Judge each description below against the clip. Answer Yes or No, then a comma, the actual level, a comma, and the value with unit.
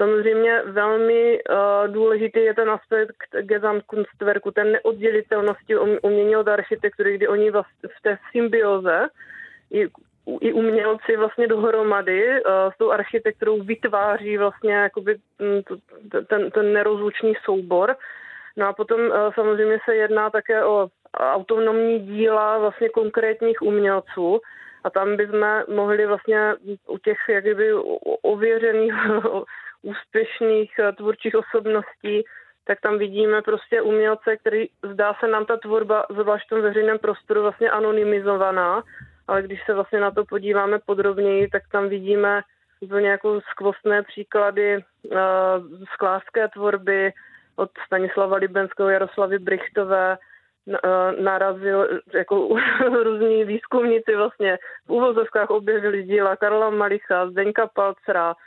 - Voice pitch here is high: Yes, high, 210 Hz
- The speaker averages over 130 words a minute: No, average, 120 wpm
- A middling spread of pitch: No, narrow, 1.8 semitones